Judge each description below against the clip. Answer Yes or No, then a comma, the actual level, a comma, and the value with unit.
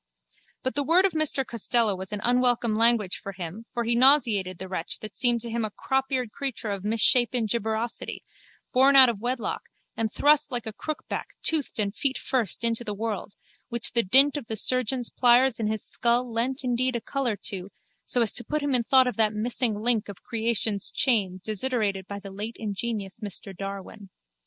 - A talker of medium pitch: No, high, 230 Hz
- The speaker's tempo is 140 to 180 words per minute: No, average, 195 wpm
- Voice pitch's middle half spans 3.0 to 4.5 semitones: Yes, average, 3.3 semitones